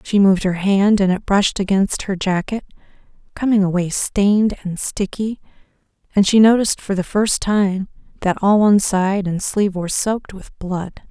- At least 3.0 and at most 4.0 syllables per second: No, 5.0 syllables/s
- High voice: Yes, high, 195 Hz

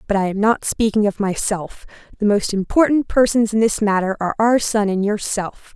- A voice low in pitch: No, high, 210 Hz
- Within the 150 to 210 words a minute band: Yes, average, 200 wpm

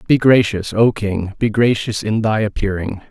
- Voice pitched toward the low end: Yes, low, 105 Hz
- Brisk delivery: No, average, 175 wpm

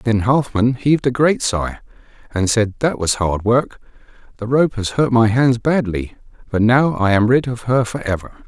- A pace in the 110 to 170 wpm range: No, average, 200 wpm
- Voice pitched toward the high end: No, low, 120 Hz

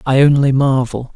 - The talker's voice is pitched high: No, low, 135 Hz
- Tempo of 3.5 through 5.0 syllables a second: Yes, 4.9 syllables/s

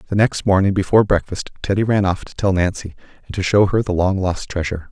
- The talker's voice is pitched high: No, very low, 95 Hz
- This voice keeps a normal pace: No, fast, 230 wpm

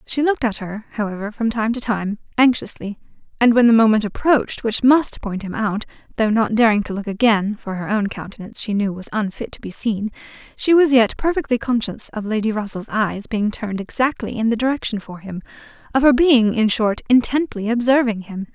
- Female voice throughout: Yes, female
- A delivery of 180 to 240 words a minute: Yes, average, 195 wpm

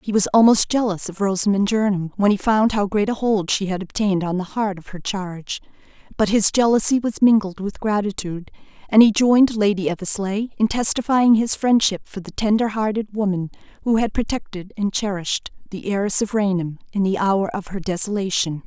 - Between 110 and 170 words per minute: No, average, 190 wpm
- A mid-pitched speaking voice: No, high, 205 Hz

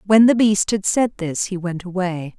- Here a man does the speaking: No, female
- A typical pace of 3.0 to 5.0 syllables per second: Yes, 4.6 syllables/s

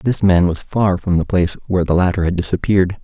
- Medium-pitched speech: No, very low, 90 Hz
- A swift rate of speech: Yes, fast, 235 wpm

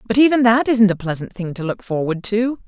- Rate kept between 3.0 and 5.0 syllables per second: No, 5.5 syllables/s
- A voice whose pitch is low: No, high, 215 Hz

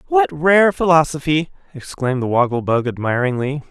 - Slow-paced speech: Yes, slow, 130 wpm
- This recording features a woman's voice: No, male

